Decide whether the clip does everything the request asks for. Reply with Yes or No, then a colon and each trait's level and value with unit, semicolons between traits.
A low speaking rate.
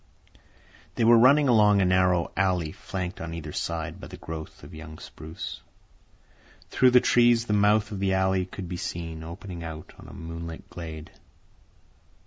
No: average, 165 wpm